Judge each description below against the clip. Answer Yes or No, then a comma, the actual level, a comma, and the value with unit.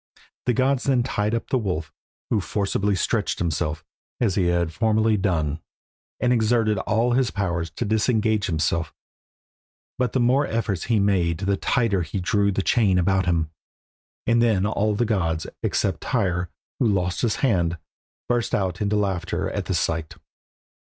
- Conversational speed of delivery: Yes, average, 160 wpm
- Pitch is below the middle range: Yes, low, 100 Hz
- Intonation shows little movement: No, average, 4.4 semitones